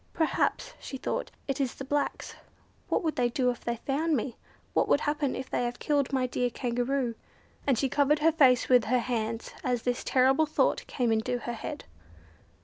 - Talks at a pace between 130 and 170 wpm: No, average, 195 wpm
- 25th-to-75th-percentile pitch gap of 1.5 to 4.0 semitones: Yes, average, 2.8 semitones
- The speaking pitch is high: Yes, very high, 255 Hz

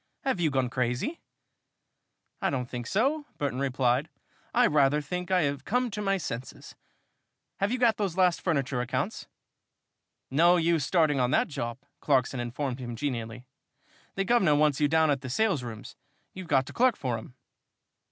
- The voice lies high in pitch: No, medium, 145 Hz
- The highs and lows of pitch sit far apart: Yes, wide, 6.5 semitones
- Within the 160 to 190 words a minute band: Yes, average, 165 wpm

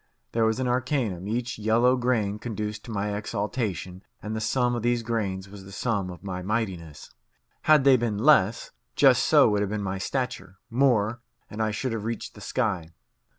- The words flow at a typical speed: Yes, average, 190 wpm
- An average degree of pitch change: Yes, average, 3.2 semitones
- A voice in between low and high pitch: No, low, 110 Hz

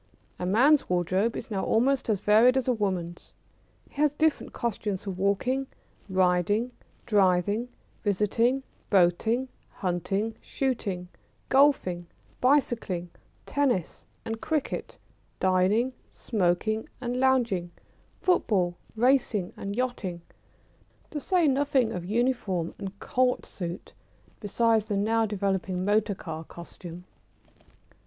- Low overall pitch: No, high, 210 Hz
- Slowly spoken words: Yes, slow, 110 wpm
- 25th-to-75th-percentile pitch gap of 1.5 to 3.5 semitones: No, average, 5.3 semitones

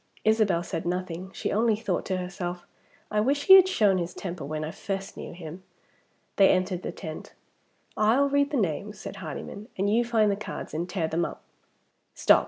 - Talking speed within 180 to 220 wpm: Yes, average, 190 wpm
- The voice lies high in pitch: Yes, high, 195 Hz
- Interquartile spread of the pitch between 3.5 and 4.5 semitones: Yes, average, 3.8 semitones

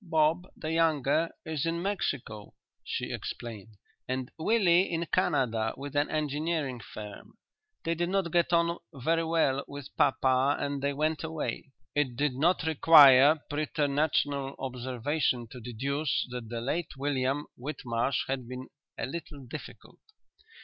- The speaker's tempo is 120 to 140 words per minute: Yes, slow, 135 wpm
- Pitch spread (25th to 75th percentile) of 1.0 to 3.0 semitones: No, average, 3.8 semitones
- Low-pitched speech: No, medium, 145 Hz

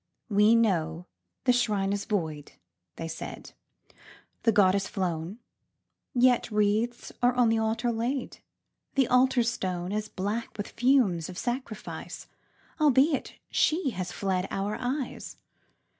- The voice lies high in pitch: Yes, high, 215 Hz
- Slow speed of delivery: Yes, slow, 125 wpm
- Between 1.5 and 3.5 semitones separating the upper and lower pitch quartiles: No, average, 4.4 semitones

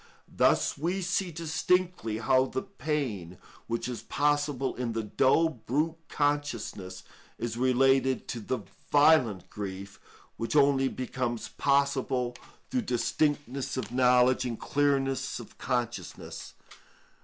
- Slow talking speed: Yes, slow, 115 wpm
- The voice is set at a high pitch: No, low, 130 Hz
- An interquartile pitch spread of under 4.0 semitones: Yes, average, 3.6 semitones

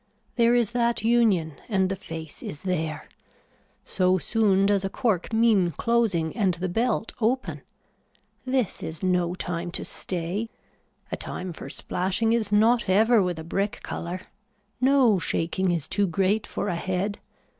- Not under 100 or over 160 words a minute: Yes, average, 155 wpm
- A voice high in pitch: Yes, high, 195 Hz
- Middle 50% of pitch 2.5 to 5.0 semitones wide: Yes, average, 4.2 semitones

